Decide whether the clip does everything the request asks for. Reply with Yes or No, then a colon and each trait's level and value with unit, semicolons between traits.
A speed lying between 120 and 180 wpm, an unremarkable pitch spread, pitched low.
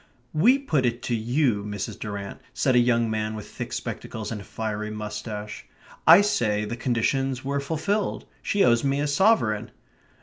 Yes: average, 170 wpm; average, 4.8 semitones; low, 120 Hz